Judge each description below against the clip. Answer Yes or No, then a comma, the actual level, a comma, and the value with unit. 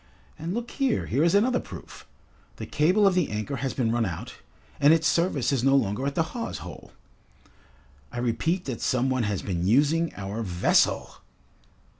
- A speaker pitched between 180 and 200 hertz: No, medium, 140 Hz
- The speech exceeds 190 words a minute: No, average, 180 wpm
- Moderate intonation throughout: No, wide, 6.7 semitones